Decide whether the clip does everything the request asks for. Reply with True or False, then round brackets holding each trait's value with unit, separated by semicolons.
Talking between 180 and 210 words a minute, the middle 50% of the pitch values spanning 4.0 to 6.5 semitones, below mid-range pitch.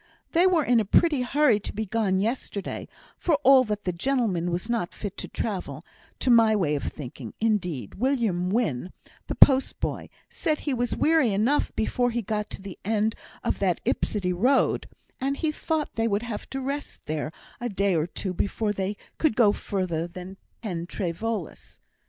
False (185 wpm; 5.2 semitones; 215 Hz)